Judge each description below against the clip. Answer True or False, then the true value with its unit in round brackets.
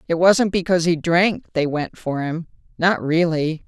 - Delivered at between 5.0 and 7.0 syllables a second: False (4.6 syllables/s)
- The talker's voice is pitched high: False (170 Hz)